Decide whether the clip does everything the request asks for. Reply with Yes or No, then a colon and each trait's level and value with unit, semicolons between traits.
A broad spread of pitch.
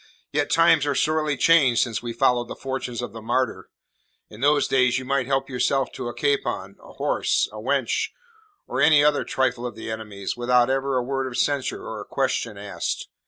No: average, 3.2 semitones